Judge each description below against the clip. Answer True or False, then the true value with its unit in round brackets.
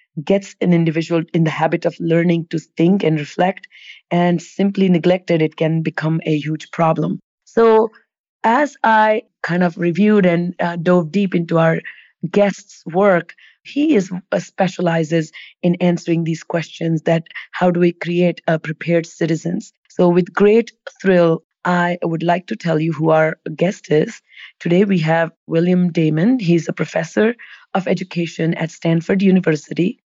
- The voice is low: False (175 Hz)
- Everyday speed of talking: True (155 wpm)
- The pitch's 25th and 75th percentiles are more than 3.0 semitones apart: False (2.5 semitones)